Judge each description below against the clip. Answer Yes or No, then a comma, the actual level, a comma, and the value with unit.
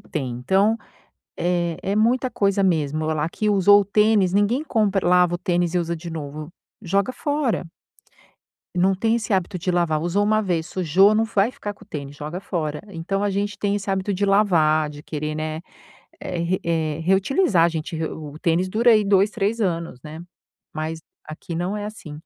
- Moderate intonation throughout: Yes, average, 4.1 semitones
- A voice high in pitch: No, medium, 180 Hz